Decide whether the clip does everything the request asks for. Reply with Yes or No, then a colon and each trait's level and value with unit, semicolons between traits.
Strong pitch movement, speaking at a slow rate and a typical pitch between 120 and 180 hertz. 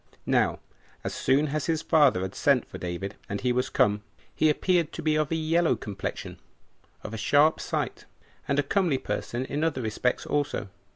No: wide, 5.8 semitones; average, 185 wpm; medium, 140 Hz